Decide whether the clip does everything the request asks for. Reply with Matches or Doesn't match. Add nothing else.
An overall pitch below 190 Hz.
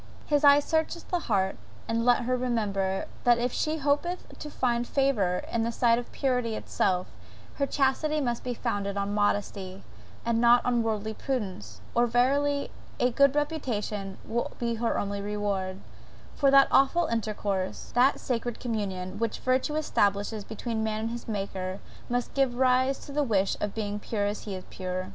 Doesn't match